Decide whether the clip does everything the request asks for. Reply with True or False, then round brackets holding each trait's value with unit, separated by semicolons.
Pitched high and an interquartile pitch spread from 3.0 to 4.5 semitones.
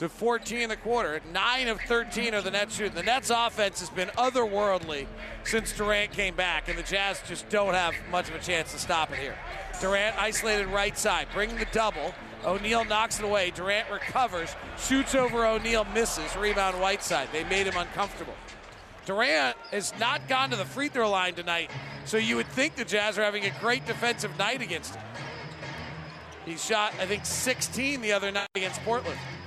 True (210 Hz; 3.3 semitones)